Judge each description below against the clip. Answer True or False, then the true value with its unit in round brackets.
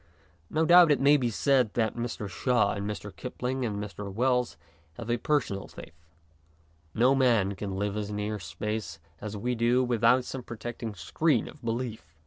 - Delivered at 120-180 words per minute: True (170 wpm)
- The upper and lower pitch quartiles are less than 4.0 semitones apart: True (3.5 semitones)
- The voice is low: True (115 Hz)